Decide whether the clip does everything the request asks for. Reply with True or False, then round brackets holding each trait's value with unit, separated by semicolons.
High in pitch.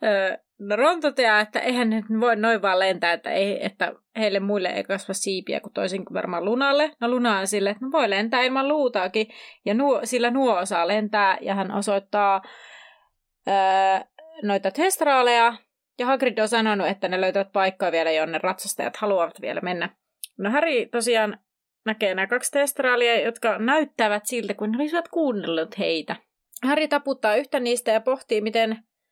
True (220 Hz)